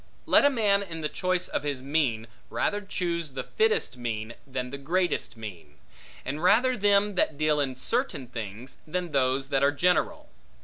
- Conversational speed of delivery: Yes, average, 175 wpm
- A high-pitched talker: No, medium, 150 Hz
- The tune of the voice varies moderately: No, wide, 6.3 semitones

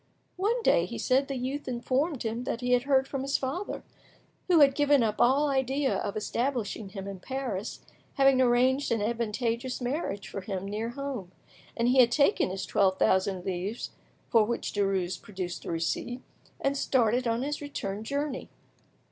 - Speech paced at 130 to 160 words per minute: No, average, 175 wpm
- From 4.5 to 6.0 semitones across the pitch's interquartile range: Yes, average, 4.8 semitones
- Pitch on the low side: No, high, 245 Hz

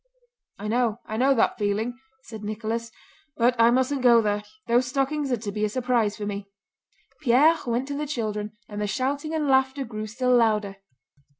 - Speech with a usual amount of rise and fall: Yes, average, 3.7 semitones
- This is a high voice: Yes, high, 235 Hz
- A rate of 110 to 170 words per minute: No, average, 180 wpm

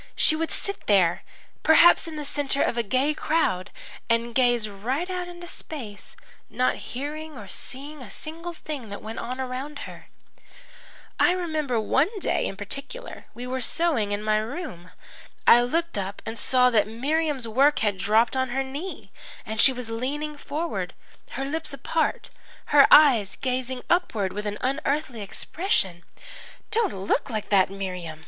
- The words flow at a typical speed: Yes, average, 160 wpm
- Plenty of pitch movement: Yes, wide, 6.0 semitones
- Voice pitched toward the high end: Yes, very high, 260 Hz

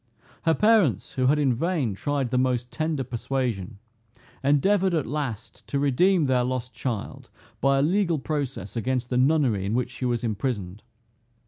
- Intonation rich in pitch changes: No, average, 3.7 semitones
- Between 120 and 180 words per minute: Yes, average, 160 wpm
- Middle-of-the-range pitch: No, low, 130 Hz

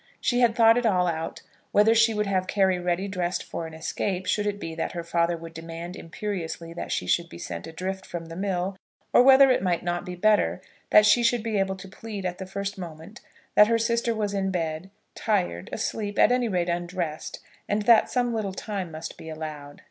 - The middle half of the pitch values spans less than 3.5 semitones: No, average, 3.9 semitones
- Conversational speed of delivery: No, fast, 215 wpm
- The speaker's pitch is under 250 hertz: Yes, high, 190 Hz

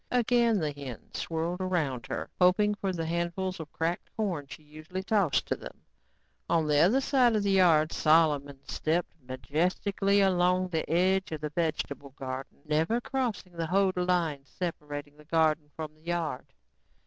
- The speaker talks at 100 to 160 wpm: Yes, average, 155 wpm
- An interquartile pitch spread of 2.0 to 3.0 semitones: No, average, 3.8 semitones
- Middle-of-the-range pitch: Yes, medium, 170 Hz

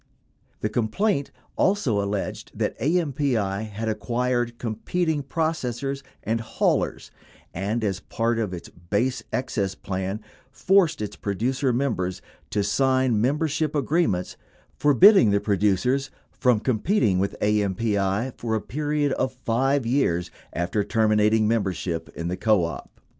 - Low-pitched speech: Yes, low, 115 Hz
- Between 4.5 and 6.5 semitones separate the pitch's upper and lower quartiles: Yes, average, 5.1 semitones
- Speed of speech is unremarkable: No, slow, 125 wpm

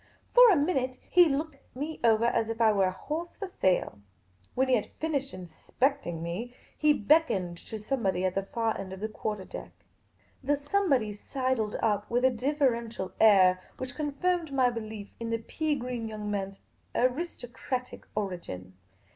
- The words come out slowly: No, average, 170 wpm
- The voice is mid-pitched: No, high, 235 Hz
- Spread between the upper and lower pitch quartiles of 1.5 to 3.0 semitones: No, wide, 5.5 semitones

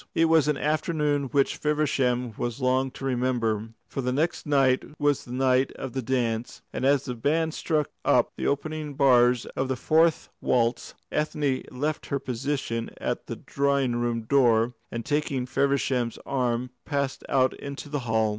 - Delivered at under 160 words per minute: No, average, 165 wpm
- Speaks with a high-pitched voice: No, low, 135 Hz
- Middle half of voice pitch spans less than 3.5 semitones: Yes, average, 2.9 semitones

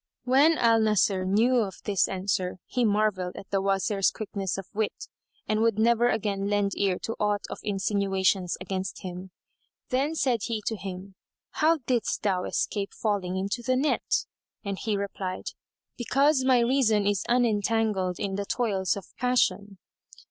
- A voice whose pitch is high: Yes, high, 205 Hz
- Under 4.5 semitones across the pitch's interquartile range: Yes, average, 3.4 semitones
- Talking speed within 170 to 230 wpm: No, average, 155 wpm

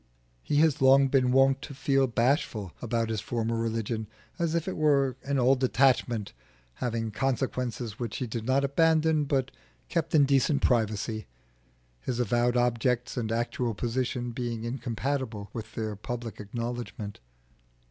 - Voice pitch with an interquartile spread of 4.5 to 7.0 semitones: No, average, 3.0 semitones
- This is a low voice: Yes, low, 120 Hz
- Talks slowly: No, average, 145 wpm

